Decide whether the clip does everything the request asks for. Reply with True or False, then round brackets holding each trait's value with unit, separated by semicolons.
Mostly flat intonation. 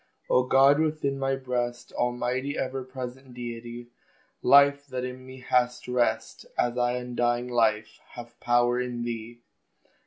True (1.4 semitones)